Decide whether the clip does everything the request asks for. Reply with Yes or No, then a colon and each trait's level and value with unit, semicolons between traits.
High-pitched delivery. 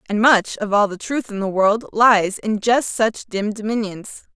Yes: high, 215 Hz